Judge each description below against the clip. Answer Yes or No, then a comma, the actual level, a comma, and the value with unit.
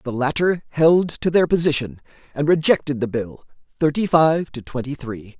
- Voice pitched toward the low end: No, medium, 145 Hz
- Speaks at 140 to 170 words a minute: Yes, average, 165 wpm